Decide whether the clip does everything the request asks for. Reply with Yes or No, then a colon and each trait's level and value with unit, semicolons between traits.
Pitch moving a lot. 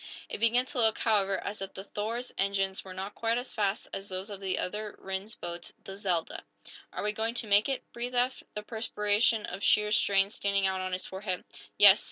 No: narrow, 2.4 semitones